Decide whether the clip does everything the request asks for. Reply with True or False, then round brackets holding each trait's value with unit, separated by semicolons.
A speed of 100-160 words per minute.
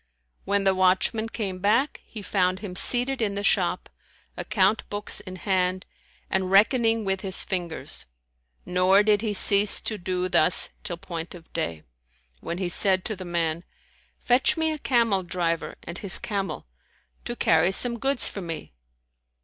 True (155 wpm)